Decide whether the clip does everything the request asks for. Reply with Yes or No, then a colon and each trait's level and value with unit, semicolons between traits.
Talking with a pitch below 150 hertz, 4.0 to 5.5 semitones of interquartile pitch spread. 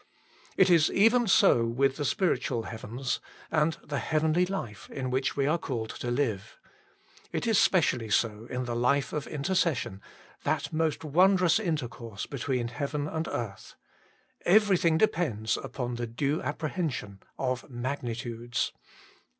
Yes: medium, 140 Hz; average, 5.2 semitones